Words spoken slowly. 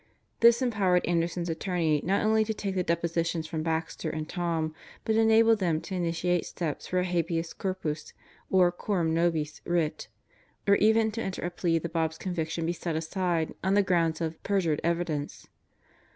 No: average, 175 wpm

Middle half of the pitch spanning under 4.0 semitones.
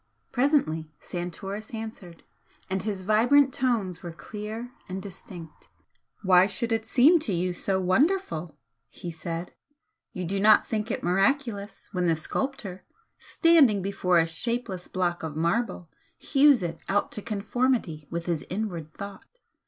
No: average, 4.8 semitones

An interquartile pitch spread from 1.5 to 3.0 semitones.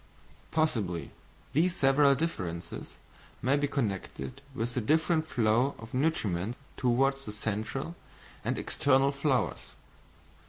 No: average, 4.6 semitones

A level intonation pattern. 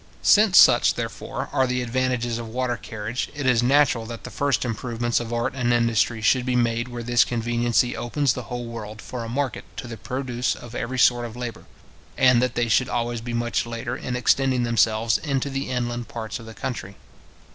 Yes: narrow, 1.5 semitones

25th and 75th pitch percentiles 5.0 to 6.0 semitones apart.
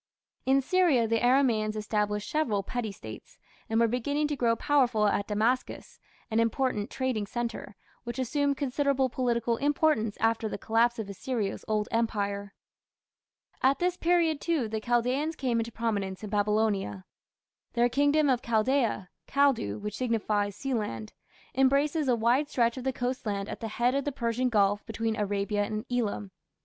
No: average, 3.8 semitones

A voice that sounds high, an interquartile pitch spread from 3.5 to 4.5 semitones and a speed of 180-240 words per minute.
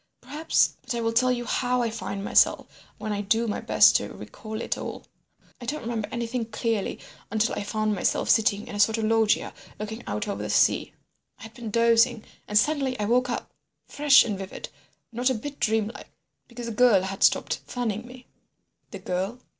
No: high, 225 Hz; narrow, 2.5 semitones; average, 185 wpm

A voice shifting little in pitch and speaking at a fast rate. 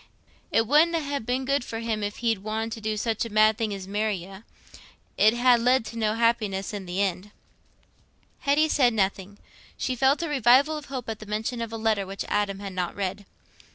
No: average, 3.4 semitones; fast, 215 wpm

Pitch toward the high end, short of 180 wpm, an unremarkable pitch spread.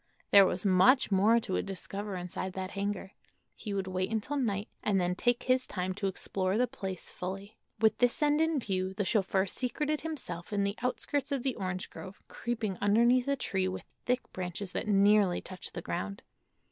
No: high, 200 Hz; average, 185 wpm; average, 4.4 semitones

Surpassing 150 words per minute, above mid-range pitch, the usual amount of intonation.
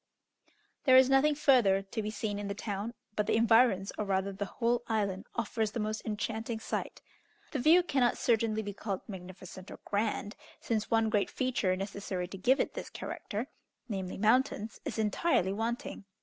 Yes: average, 175 wpm; high, 215 Hz; average, 3.1 semitones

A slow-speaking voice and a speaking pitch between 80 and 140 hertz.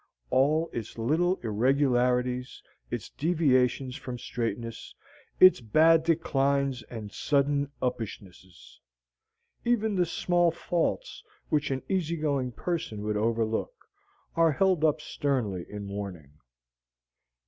Yes: slow, 105 wpm; low, 135 Hz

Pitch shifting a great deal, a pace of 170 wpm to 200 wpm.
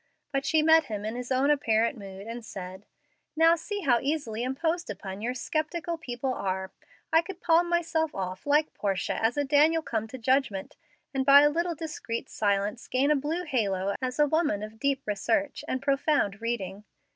Yes: wide, 6.2 semitones; average, 185 wpm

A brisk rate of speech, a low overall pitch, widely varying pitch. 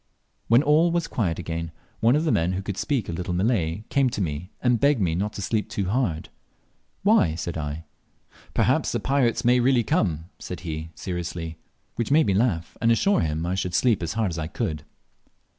Yes: fast, 210 wpm; very low, 95 Hz; wide, 6.6 semitones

